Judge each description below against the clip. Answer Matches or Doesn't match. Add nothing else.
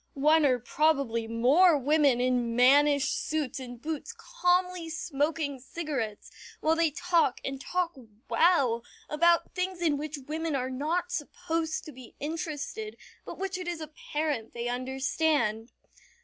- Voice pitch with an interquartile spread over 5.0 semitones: Doesn't match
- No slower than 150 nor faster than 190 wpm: Doesn't match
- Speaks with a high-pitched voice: Matches